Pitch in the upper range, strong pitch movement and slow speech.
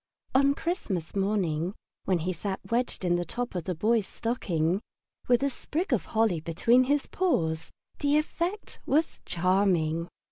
No: high, 200 Hz; wide, 7.0 semitones; average, 150 wpm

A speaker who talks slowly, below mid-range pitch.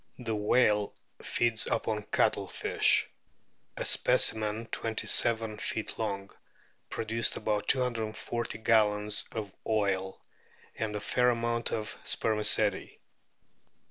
Yes: slow, 100 wpm; low, 110 Hz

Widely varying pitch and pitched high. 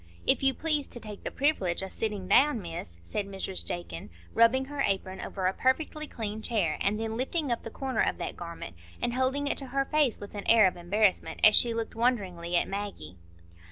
Yes: wide, 5.7 semitones; high, 215 Hz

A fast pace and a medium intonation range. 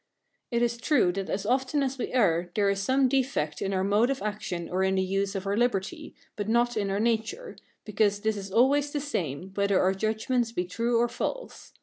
Yes: fast, 220 wpm; average, 4.3 semitones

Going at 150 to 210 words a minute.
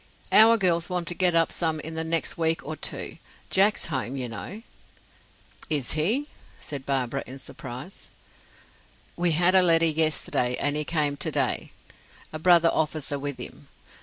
Yes: average, 165 wpm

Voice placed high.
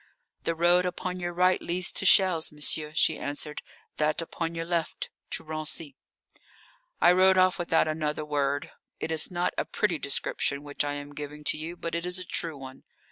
No: medium, 165 Hz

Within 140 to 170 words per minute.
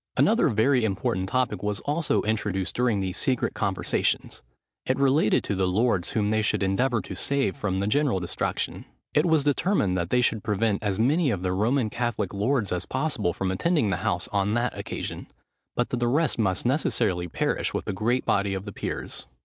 No: average, 195 wpm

